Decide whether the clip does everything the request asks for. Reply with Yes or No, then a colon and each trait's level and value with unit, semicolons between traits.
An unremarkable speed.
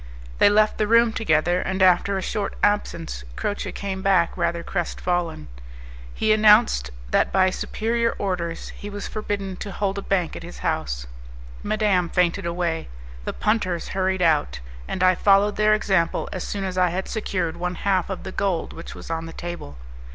Yes: average, 175 wpm